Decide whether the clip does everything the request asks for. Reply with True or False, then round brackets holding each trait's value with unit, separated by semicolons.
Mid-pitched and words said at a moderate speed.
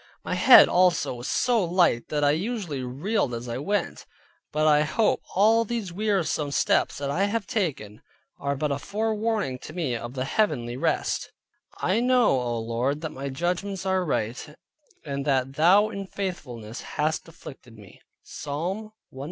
True (155 Hz; 165 wpm)